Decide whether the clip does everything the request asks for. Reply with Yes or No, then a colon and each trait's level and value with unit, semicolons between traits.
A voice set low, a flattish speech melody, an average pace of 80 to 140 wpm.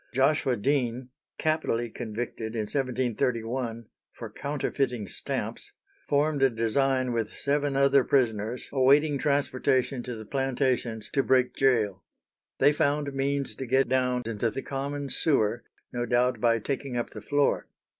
No: low, 130 Hz; average, 3.0 semitones; slow, 135 wpm